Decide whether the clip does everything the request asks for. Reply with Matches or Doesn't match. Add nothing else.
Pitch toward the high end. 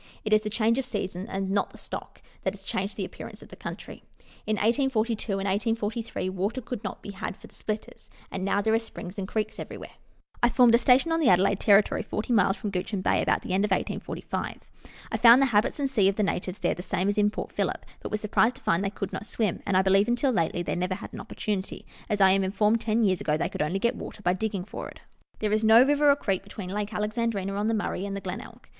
Matches